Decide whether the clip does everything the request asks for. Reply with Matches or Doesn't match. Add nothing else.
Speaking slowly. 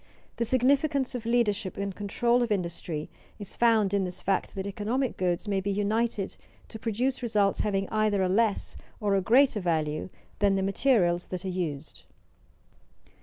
Doesn't match